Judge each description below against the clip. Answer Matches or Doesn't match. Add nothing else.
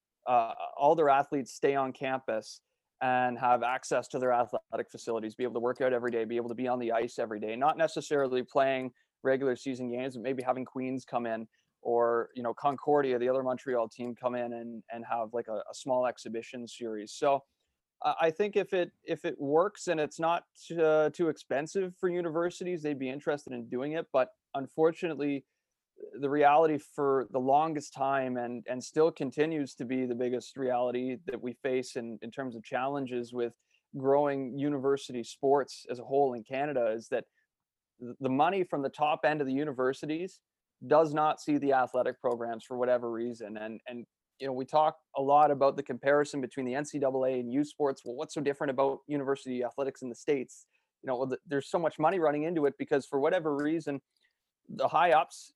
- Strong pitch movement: Doesn't match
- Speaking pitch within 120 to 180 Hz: Matches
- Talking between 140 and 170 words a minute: Doesn't match